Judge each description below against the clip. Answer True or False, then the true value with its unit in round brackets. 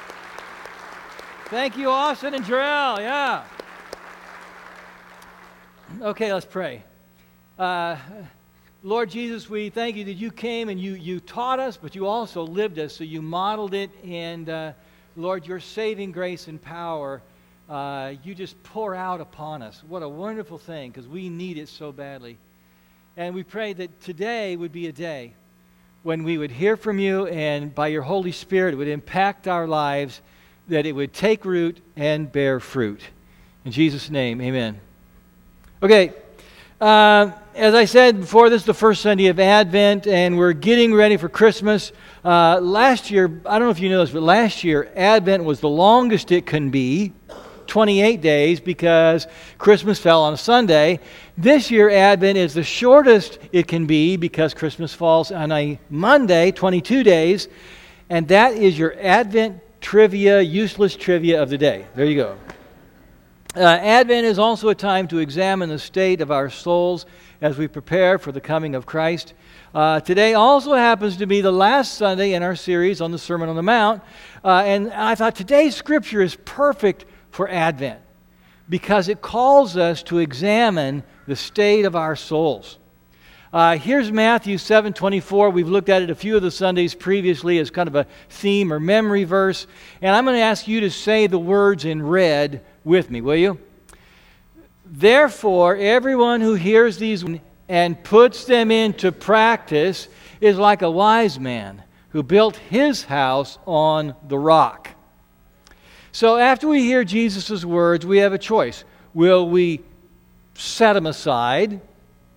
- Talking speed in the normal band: True (165 wpm)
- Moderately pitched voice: True (180 Hz)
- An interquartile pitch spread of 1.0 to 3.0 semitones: False (5.3 semitones)